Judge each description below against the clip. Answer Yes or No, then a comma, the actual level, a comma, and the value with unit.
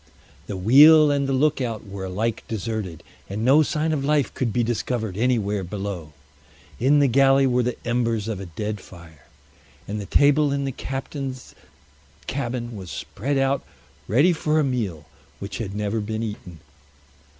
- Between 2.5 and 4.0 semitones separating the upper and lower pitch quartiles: No, average, 5.1 semitones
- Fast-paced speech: No, average, 160 wpm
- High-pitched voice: No, low, 120 Hz